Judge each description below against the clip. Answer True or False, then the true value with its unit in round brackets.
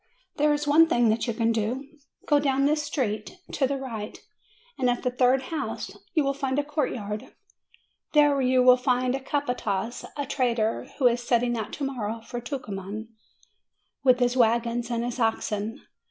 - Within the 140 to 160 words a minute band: False (175 wpm)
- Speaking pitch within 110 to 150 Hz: False (250 Hz)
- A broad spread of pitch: False (3.2 semitones)